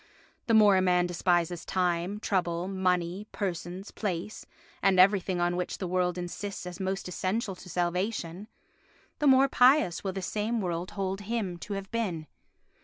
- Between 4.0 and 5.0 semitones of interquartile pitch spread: No, narrow, 2.5 semitones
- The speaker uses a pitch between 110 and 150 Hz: No, medium, 185 Hz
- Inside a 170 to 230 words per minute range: No, average, 160 wpm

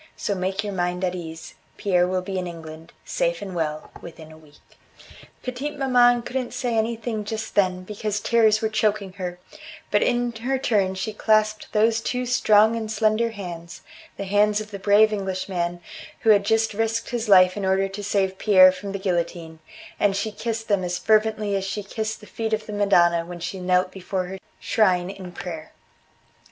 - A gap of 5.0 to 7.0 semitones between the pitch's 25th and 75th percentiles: No, average, 3.1 semitones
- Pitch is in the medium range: No, high, 200 Hz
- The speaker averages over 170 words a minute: Yes, average, 190 wpm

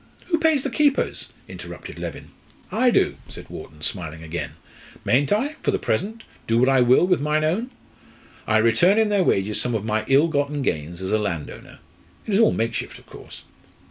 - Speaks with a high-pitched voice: No, medium, 140 Hz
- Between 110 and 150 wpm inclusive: No, average, 190 wpm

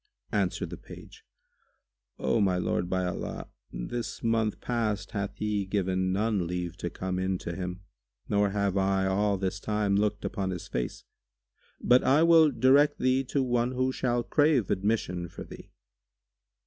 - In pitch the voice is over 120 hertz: No, low, 100 Hz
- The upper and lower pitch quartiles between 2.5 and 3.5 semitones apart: No, average, 4.3 semitones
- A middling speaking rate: Yes, average, 160 wpm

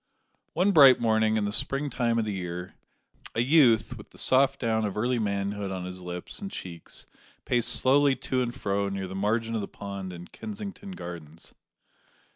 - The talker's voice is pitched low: Yes, low, 110 Hz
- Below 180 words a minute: No, average, 185 wpm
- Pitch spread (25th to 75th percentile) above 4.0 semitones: Yes, average, 4.9 semitones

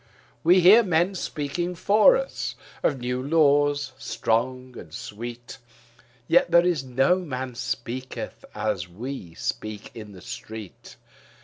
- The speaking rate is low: Yes, slow, 125 wpm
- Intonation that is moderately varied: No, wide, 6.4 semitones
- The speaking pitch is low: Yes, low, 130 Hz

